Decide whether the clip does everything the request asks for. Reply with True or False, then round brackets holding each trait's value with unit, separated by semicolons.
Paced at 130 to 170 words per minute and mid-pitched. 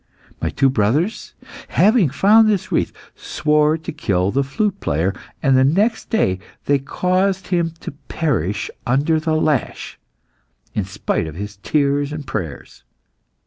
True (145 wpm; 145 Hz)